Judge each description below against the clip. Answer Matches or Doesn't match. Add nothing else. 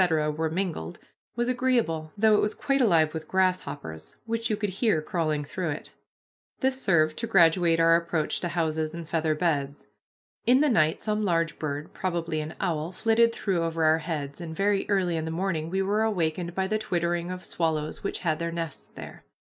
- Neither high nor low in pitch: Matches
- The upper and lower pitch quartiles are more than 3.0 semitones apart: Matches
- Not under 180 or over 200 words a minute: Matches